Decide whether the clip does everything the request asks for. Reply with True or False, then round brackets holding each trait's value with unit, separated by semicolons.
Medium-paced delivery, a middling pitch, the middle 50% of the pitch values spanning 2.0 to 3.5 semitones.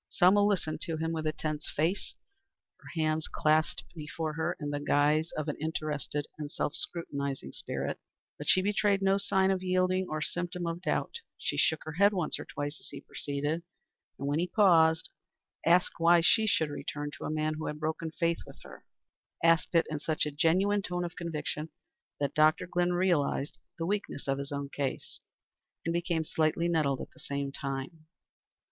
True (185 wpm; 160 Hz; 2.9 semitones)